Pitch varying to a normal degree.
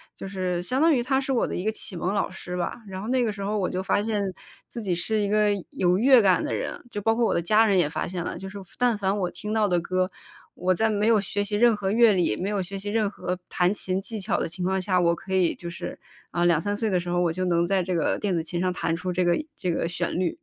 Yes: average, 3.1 semitones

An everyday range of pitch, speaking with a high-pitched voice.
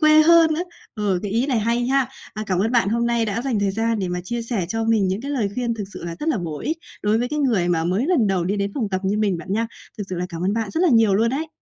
Yes: average, 4.3 semitones; high, 225 Hz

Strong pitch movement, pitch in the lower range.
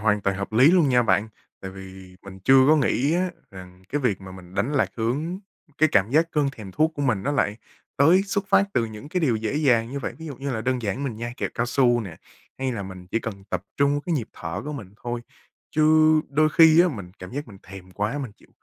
Yes: wide, 6.5 semitones; low, 120 Hz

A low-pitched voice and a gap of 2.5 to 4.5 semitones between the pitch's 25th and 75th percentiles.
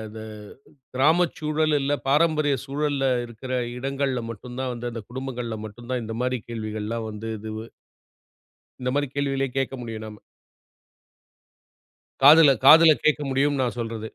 Yes: low, 130 Hz; average, 3.8 semitones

